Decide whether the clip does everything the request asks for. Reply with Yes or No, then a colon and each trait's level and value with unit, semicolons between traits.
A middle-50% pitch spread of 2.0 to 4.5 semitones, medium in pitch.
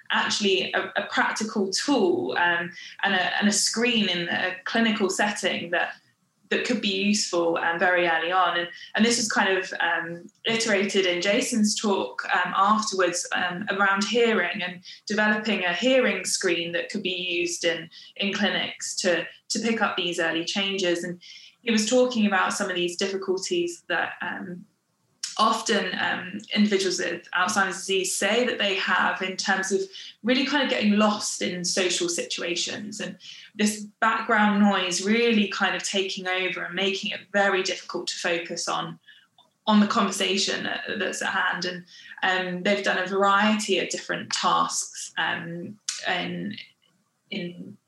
No: average, 2.9 semitones; high, 195 Hz